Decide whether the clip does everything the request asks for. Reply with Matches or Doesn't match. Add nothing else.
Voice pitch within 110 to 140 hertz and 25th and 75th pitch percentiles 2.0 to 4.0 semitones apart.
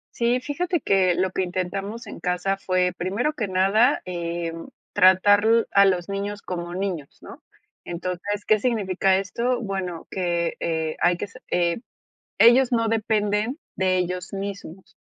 Doesn't match